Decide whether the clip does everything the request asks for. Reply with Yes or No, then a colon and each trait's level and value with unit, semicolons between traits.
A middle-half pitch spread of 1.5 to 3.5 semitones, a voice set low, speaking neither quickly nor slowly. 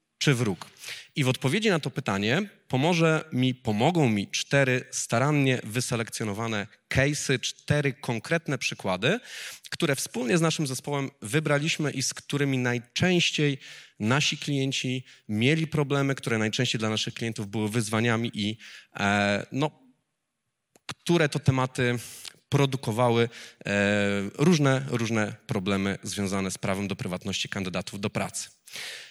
No: average, 5.0 semitones; low, 130 Hz; average, 120 wpm